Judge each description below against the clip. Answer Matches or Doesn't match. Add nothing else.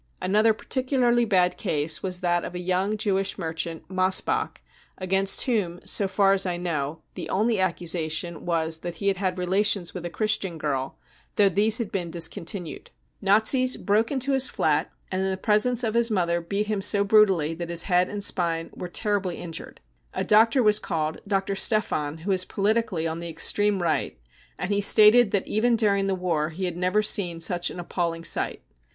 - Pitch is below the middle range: Doesn't match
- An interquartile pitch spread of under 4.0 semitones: Matches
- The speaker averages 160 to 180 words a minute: Doesn't match